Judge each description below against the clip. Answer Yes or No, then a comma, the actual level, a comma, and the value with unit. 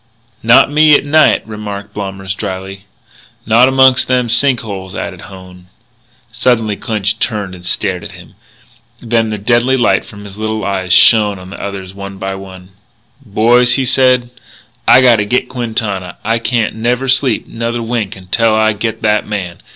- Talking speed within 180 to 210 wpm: No, average, 165 wpm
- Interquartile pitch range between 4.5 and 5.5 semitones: No, average, 3.7 semitones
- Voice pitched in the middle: No, low, 110 Hz